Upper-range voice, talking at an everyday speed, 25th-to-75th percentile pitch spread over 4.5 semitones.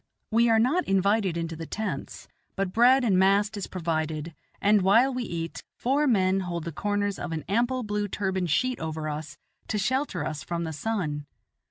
Yes: high, 195 Hz; average, 185 wpm; average, 5.1 semitones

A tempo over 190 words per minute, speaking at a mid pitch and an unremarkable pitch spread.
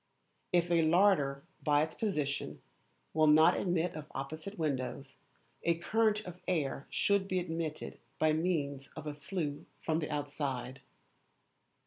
No: slow, 135 wpm; medium, 155 Hz; average, 3.5 semitones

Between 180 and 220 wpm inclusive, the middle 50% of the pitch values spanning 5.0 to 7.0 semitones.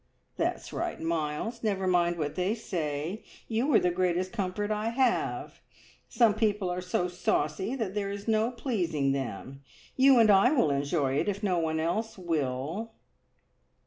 No: average, 155 wpm; average, 5.3 semitones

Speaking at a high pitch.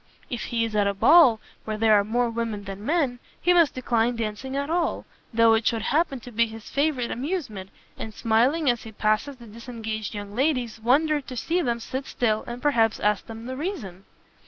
Yes: high, 235 Hz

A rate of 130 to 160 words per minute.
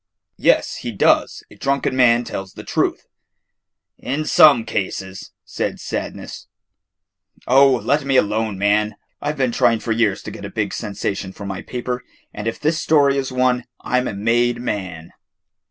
No: average, 170 wpm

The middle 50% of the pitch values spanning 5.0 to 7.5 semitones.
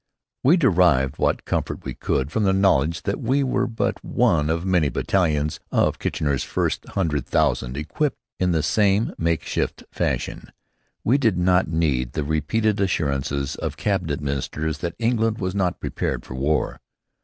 Yes: wide, 5.4 semitones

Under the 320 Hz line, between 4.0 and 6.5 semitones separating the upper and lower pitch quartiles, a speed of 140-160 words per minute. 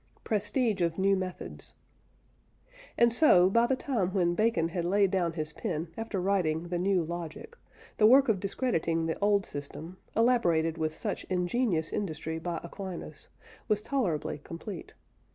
Yes: medium, 185 Hz; average, 4.3 semitones; average, 150 wpm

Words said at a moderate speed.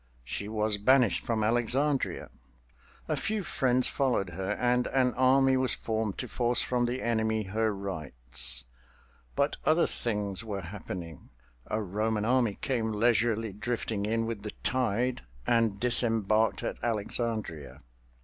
No: slow, 130 wpm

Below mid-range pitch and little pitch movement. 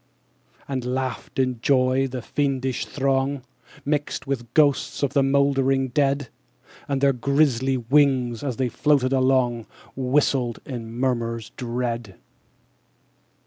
Yes: low, 130 Hz; narrow, 2.1 semitones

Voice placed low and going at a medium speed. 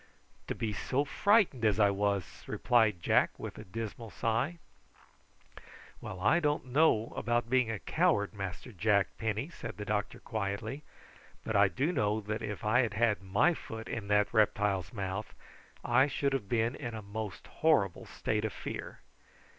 Yes: low, 110 Hz; average, 165 wpm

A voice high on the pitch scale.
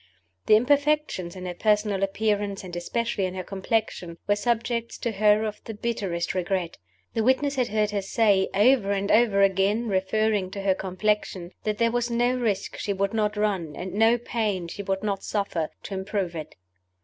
Yes: high, 205 Hz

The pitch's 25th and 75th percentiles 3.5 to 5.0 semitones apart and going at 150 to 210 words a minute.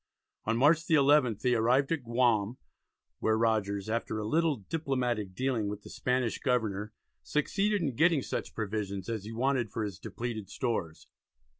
Yes: average, 4.2 semitones; average, 160 wpm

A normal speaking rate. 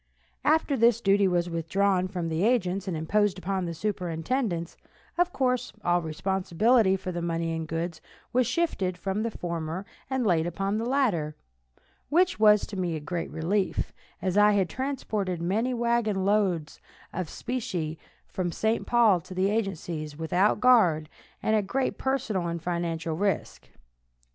Yes: average, 155 wpm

